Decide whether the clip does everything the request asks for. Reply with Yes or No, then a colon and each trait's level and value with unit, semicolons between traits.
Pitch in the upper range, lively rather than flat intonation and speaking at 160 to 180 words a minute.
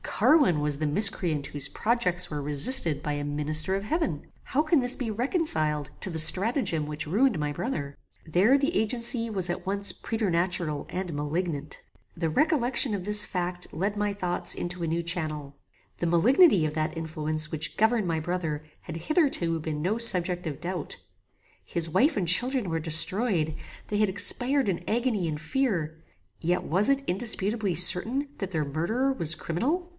No: medium, 180 Hz; wide, 6.3 semitones; average, 170 wpm